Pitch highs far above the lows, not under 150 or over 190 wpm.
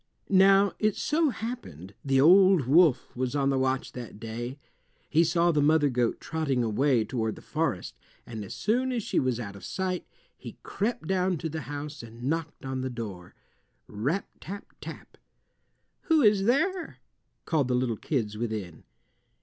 Yes: wide, 7.8 semitones; average, 165 wpm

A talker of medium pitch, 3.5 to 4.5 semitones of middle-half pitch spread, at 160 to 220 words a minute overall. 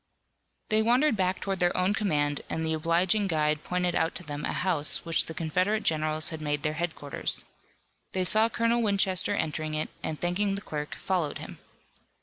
Yes: medium, 175 Hz; average, 4.1 semitones; average, 180 wpm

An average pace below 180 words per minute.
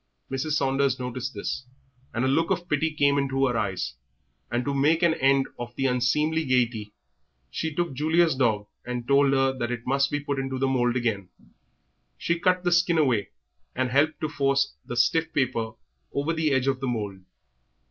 No: average, 190 wpm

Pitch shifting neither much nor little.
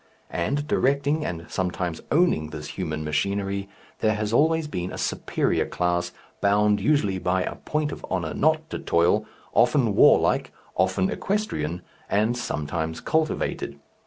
No: wide, 8.5 semitones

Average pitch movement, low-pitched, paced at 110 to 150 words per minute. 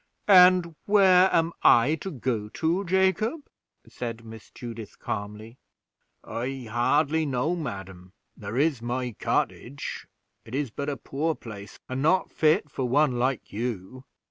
No: wide, 5.8 semitones; low, 130 Hz; average, 140 wpm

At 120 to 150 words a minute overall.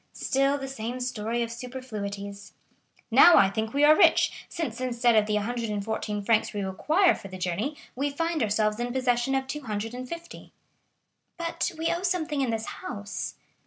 No: average, 160 wpm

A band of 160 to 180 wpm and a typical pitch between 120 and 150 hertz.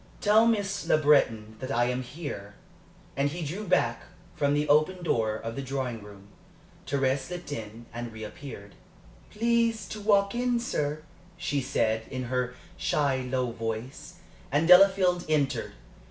No: average, 150 wpm; medium, 140 Hz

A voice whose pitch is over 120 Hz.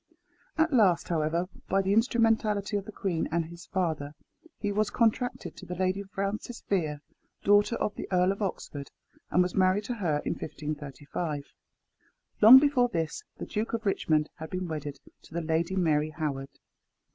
Yes: medium, 185 Hz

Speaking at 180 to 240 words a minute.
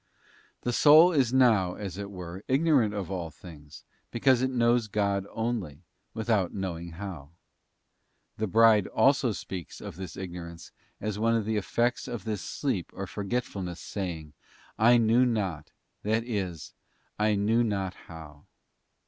No: average, 145 wpm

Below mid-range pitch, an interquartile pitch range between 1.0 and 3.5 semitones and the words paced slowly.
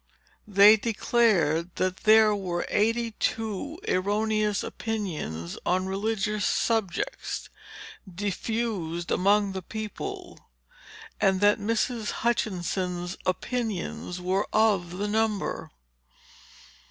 No: high, 205 Hz; average, 3.2 semitones; slow, 90 wpm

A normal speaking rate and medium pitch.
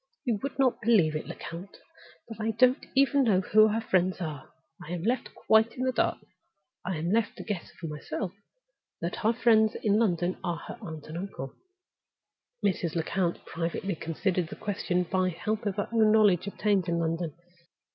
No: average, 185 wpm; high, 195 Hz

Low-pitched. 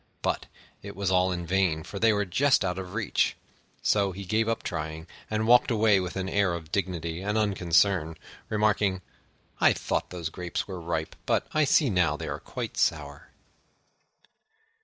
Yes: very low, 95 Hz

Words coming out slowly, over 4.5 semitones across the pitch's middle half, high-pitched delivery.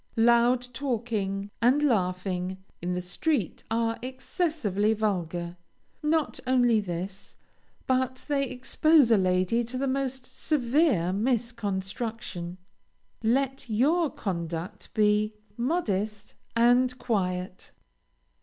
Yes: slow, 100 wpm; average, 5.1 semitones; high, 230 Hz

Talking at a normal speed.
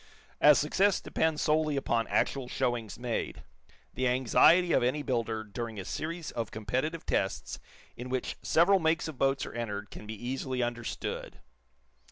Yes: average, 155 wpm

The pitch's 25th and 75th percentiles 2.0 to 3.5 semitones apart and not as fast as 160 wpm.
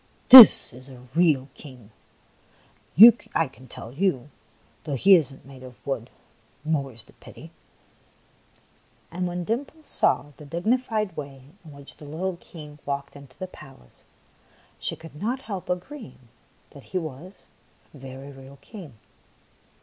No: average, 5.3 semitones; average, 150 wpm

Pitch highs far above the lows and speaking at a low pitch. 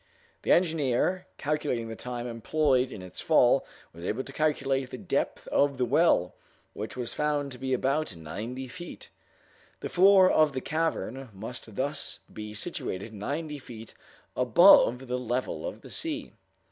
No: average, 4.6 semitones; low, 130 Hz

